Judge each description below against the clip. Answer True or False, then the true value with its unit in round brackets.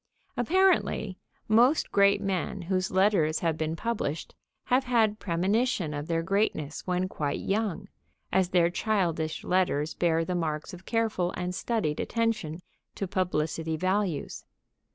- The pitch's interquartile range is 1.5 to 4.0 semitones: False (4.6 semitones)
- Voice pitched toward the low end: False (185 Hz)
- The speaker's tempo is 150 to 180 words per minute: False (135 wpm)